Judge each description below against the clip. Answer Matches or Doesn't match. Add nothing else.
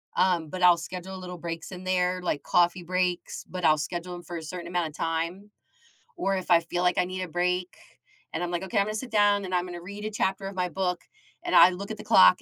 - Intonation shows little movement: Matches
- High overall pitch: Doesn't match